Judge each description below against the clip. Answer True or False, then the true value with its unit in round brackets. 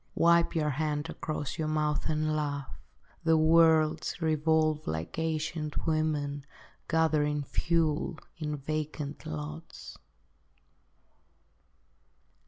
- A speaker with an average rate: False (90 wpm)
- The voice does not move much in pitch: True (1.4 semitones)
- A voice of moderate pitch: True (155 Hz)